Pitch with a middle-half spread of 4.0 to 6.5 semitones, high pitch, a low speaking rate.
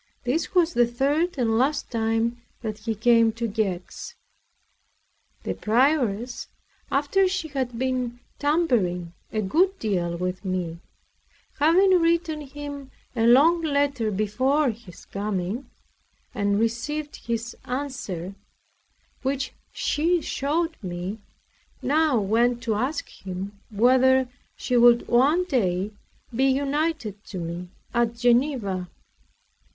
Yes: average, 5.3 semitones; high, 240 Hz; slow, 115 wpm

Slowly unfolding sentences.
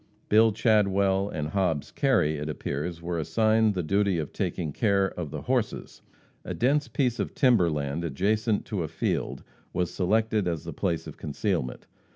No: average, 170 wpm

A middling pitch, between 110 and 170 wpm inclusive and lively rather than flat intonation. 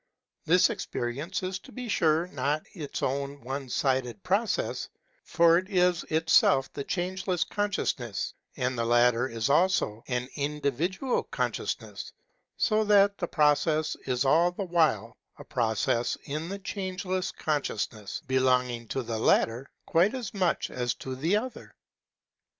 Yes: medium, 150 Hz; average, 140 wpm; wide, 6.6 semitones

